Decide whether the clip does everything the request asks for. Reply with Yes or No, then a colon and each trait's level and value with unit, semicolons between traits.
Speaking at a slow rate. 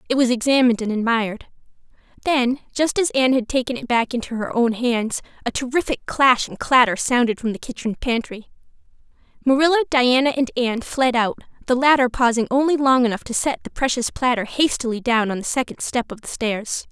No: average, 190 wpm